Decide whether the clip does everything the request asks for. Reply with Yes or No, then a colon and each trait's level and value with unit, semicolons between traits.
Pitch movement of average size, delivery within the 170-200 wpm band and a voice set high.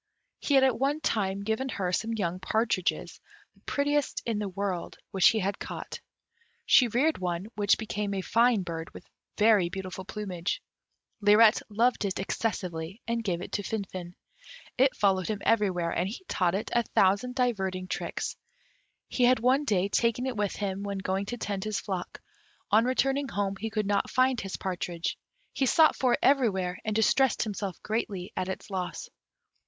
Yes: average, 3.8 semitones; average, 175 wpm; high, 205 Hz